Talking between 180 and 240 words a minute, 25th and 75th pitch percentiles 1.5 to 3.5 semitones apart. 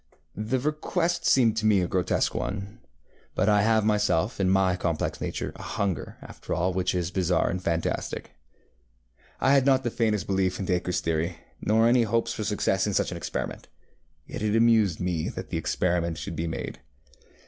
No: average, 185 wpm; average, 3.9 semitones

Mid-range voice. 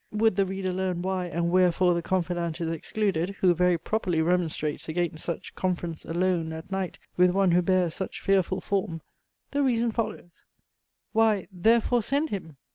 Yes: medium, 180 Hz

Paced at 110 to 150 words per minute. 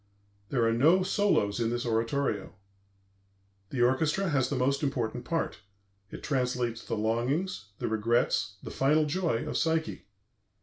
Yes: average, 140 wpm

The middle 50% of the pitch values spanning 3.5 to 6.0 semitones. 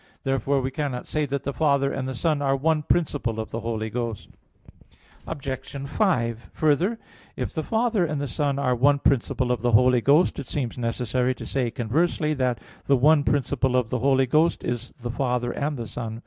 No: average, 3.1 semitones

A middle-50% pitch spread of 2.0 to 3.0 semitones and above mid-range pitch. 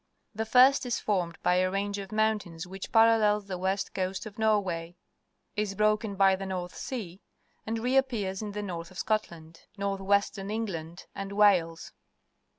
Yes: average, 2.7 semitones; high, 200 Hz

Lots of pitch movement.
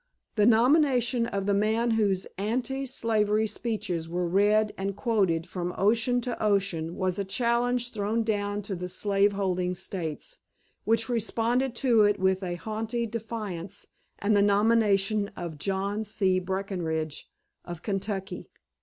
No: average, 3.2 semitones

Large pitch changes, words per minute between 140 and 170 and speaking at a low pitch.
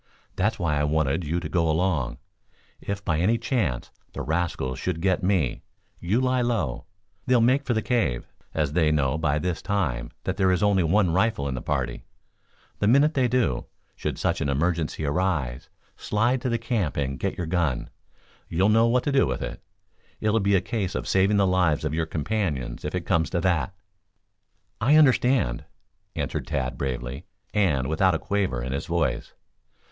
No: wide, 6.3 semitones; average, 185 wpm; very low, 90 Hz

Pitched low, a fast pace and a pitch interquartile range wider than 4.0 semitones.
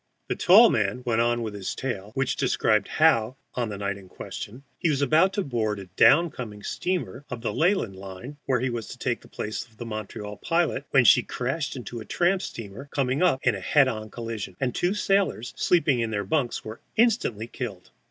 Yes: low, 120 Hz; fast, 210 wpm; average, 5.1 semitones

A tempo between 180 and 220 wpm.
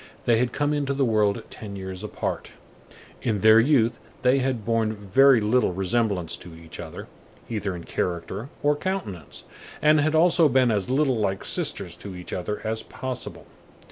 No: average, 170 wpm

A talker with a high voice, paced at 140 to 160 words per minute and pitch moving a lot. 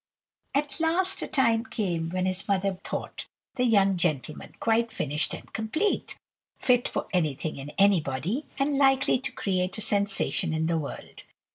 Yes: high, 200 Hz; average, 155 wpm; wide, 6.8 semitones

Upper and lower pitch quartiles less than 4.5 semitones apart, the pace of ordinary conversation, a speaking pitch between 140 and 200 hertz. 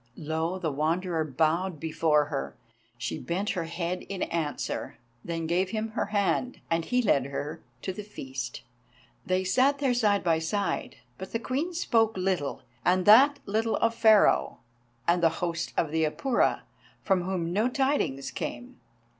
No: average, 5.2 semitones; average, 160 wpm; medium, 185 Hz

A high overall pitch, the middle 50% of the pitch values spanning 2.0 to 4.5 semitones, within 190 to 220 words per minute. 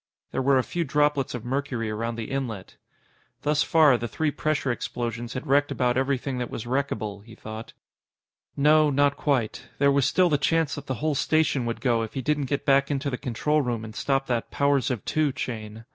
No: low, 135 Hz; average, 3.4 semitones; fast, 205 wpm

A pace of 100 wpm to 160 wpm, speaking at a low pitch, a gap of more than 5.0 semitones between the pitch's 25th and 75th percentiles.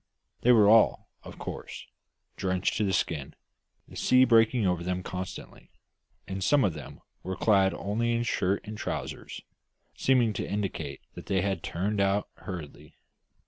No: average, 155 wpm; low, 100 Hz; average, 3.4 semitones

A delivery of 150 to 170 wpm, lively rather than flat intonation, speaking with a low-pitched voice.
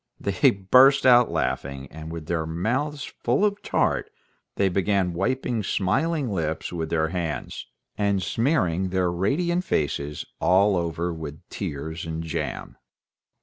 No: average, 140 wpm; wide, 7.2 semitones; very low, 95 Hz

